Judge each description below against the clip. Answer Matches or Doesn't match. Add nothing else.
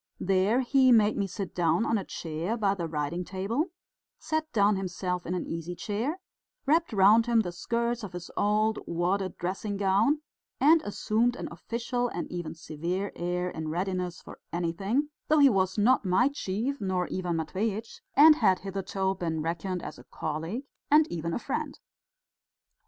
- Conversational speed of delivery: Matches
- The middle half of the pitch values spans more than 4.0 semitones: Matches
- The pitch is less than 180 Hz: Doesn't match